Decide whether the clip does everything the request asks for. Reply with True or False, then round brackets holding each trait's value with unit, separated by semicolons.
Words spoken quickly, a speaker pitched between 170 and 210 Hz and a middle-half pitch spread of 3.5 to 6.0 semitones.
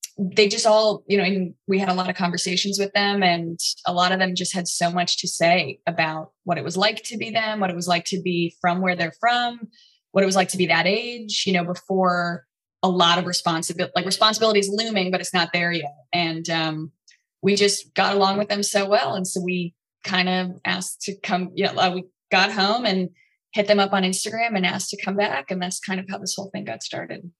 False (250 wpm; 185 Hz; 2.4 semitones)